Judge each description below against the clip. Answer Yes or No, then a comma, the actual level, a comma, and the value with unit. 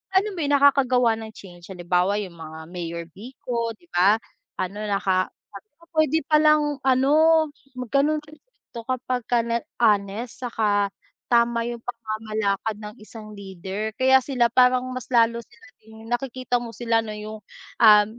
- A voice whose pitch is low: No, high, 230 Hz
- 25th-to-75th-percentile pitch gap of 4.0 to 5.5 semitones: No, average, 3.6 semitones